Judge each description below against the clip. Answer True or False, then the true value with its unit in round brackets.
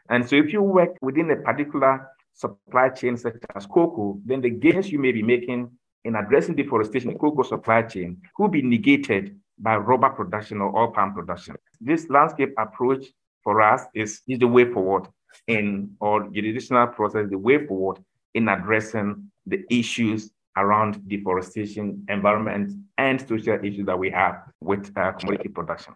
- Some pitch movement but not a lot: True (4.2 semitones)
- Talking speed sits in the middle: True (165 wpm)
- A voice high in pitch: False (115 Hz)